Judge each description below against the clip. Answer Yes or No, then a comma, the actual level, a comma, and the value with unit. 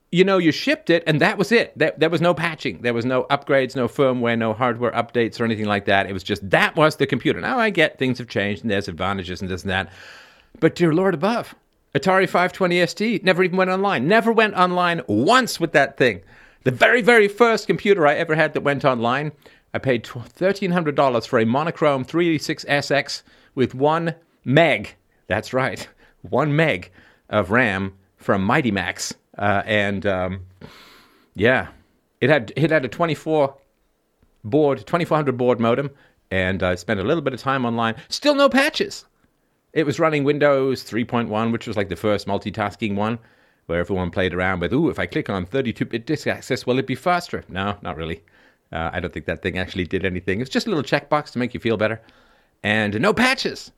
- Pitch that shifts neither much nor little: No, wide, 8.1 semitones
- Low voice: Yes, low, 130 Hz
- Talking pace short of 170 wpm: No, average, 195 wpm